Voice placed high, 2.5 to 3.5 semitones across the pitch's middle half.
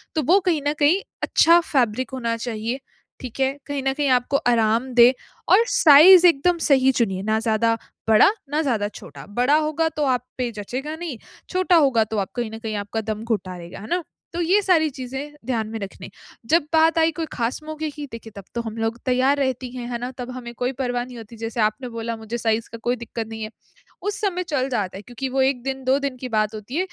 No: very high, 250 Hz; average, 4.6 semitones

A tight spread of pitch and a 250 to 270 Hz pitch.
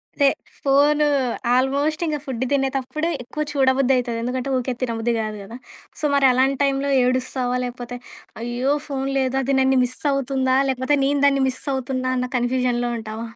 Yes: narrow, 1.8 semitones; very high, 260 Hz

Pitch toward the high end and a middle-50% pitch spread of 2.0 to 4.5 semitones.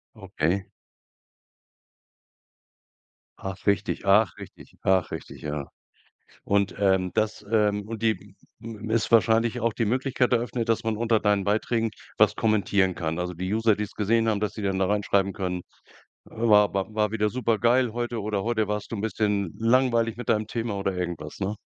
No: low, 105 Hz; narrow, 2.6 semitones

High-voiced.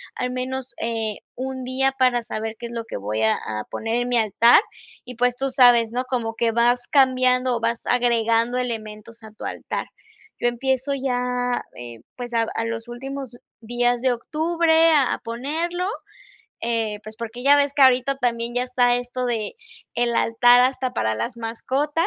Yes: high, 245 Hz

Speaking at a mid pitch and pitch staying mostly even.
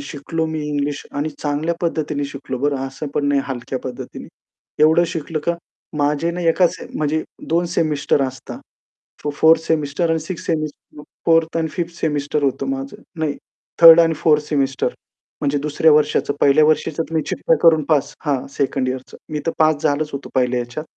Yes: medium, 150 Hz; narrow, 2.3 semitones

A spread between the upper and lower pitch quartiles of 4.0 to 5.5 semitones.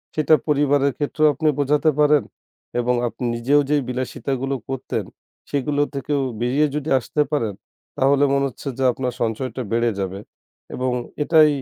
No: average, 2.8 semitones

